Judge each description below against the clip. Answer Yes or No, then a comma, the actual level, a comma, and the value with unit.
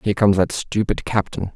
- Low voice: Yes, low, 100 Hz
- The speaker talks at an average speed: Yes, average, 195 wpm